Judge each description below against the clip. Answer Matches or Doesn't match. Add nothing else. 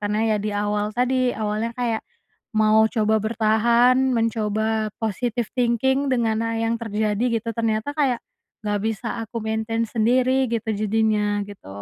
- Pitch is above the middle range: Matches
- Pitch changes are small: Matches